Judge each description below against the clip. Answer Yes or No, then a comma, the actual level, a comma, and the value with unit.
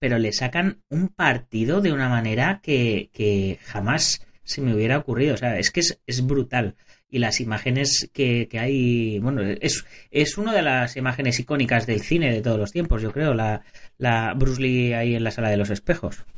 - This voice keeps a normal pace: No, fast, 200 wpm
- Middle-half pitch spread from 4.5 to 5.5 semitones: No, average, 3.6 semitones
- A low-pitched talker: Yes, low, 125 Hz